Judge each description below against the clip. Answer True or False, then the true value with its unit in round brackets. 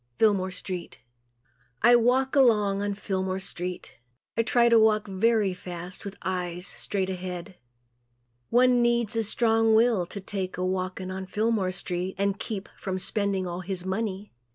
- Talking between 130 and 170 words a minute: True (155 wpm)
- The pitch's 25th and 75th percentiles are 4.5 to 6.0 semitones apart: False (3.2 semitones)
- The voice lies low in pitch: False (195 Hz)